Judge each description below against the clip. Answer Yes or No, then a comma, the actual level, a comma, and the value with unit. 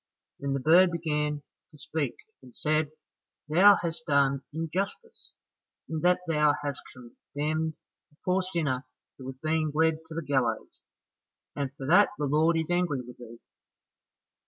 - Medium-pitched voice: Yes, medium, 155 Hz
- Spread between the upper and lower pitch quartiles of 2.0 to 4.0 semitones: Yes, average, 2.8 semitones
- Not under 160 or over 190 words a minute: No, average, 150 wpm